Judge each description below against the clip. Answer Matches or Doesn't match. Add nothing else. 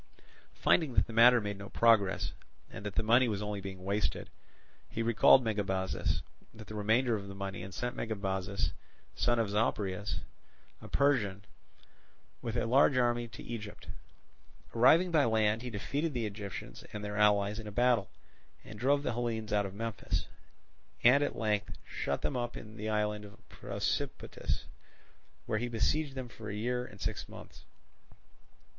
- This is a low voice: Matches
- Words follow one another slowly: Doesn't match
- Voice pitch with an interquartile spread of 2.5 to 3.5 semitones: Matches